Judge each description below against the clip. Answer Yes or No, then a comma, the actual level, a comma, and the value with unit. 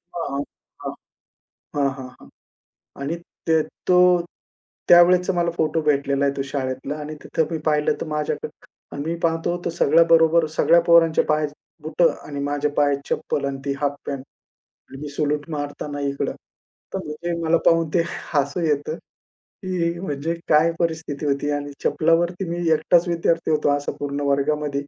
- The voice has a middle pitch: Yes, medium, 150 Hz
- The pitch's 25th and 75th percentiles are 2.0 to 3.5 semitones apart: Yes, average, 2.8 semitones